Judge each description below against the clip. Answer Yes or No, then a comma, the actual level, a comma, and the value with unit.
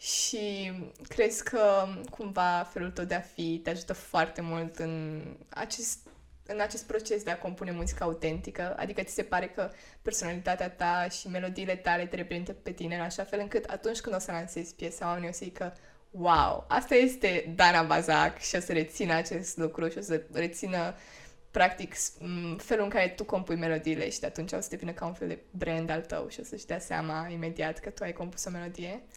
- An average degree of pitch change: Yes, average, 3.0 semitones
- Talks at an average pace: No, fast, 200 wpm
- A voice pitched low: No, medium, 175 Hz